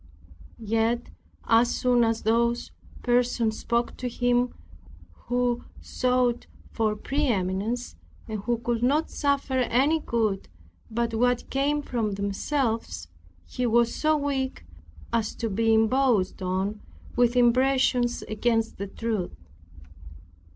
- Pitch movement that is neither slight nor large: No, narrow, 2.1 semitones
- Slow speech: Yes, slow, 115 wpm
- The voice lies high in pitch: Yes, high, 235 Hz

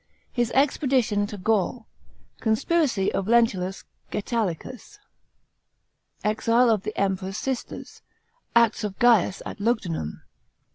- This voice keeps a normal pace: No, slow, 100 wpm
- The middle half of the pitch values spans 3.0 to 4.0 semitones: Yes, average, 3.6 semitones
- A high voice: Yes, high, 220 Hz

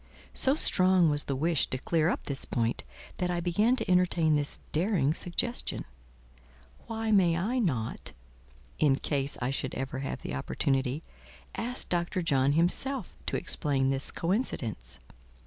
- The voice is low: No, medium, 165 Hz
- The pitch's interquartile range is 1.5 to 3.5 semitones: No, average, 5.3 semitones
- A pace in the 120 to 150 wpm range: Yes, average, 145 wpm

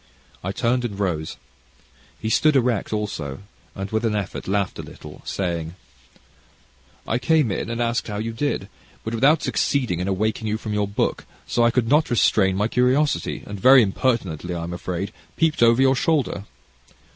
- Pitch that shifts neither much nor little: Yes, average, 4.3 semitones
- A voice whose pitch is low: Yes, low, 110 Hz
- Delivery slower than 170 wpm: No, average, 175 wpm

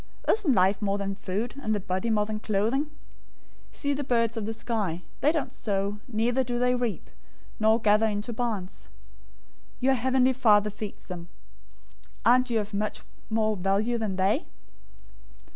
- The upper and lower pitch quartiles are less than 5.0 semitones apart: Yes, average, 3.2 semitones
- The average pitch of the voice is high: Yes, high, 220 Hz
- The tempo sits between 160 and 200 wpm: Yes, average, 165 wpm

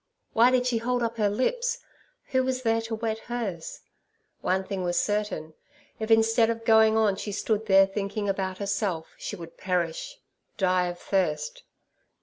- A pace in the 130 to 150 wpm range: No, average, 160 wpm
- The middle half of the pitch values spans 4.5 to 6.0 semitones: No, average, 3.3 semitones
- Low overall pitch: No, high, 215 Hz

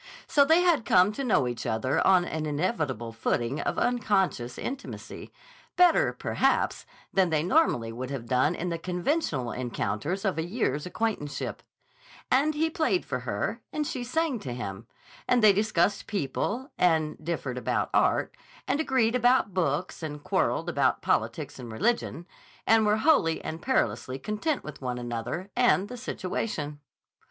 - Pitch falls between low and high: Yes, medium, 180 Hz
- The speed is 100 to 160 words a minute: Yes, average, 155 wpm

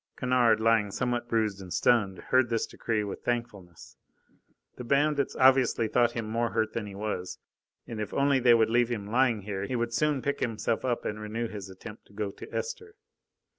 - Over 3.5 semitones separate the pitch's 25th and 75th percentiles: No, average, 2.8 semitones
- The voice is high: No, low, 115 Hz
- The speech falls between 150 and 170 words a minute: No, average, 195 wpm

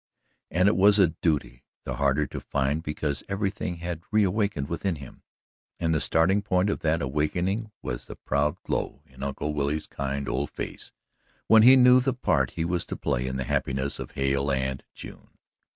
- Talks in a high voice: No, very low, 80 Hz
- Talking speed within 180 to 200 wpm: Yes, average, 185 wpm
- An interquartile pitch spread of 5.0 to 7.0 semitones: Yes, wide, 5.5 semitones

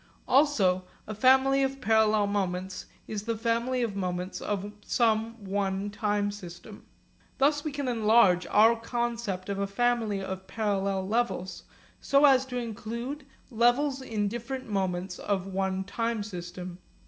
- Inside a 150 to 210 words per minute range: No, average, 140 wpm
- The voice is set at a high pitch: Yes, high, 215 Hz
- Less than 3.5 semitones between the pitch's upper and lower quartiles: No, average, 3.8 semitones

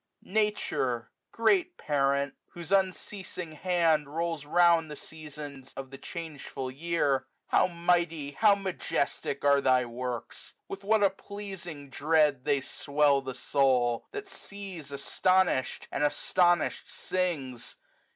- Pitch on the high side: No, medium, 155 Hz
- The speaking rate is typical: No, slow, 120 wpm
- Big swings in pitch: No, average, 4.8 semitones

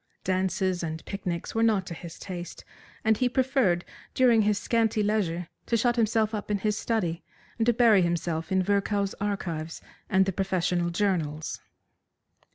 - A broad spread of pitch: No, average, 3.9 semitones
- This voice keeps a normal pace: Yes, average, 160 wpm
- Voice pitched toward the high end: Yes, high, 195 Hz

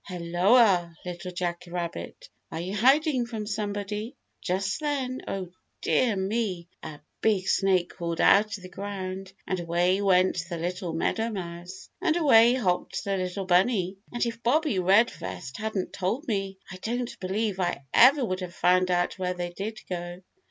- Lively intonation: No, average, 3.8 semitones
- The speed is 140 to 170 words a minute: Yes, average, 160 wpm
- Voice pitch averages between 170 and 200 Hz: Yes, high, 190 Hz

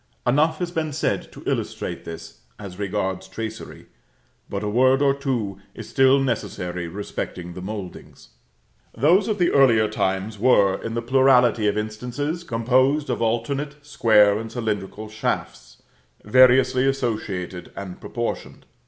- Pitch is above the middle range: No, low, 115 Hz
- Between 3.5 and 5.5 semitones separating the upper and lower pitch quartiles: Yes, average, 4.7 semitones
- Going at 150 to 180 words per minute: No, slow, 135 wpm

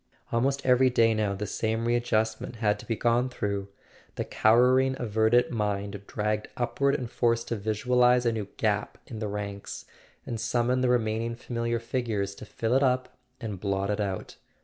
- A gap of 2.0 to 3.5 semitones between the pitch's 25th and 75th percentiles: Yes, average, 2.7 semitones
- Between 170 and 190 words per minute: Yes, average, 175 wpm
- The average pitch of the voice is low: Yes, low, 115 Hz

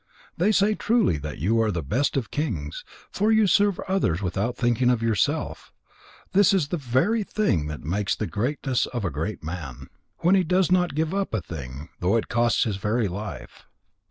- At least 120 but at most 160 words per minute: No, average, 190 wpm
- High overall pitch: No, low, 120 Hz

